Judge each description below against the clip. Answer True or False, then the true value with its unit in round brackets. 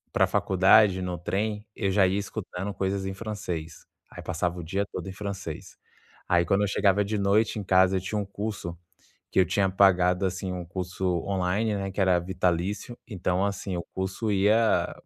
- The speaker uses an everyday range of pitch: False (1.9 semitones)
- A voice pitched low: True (95 Hz)